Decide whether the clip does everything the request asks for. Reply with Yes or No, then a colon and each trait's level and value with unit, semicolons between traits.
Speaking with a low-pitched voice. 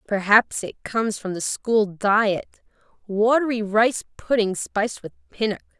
No: high, 215 Hz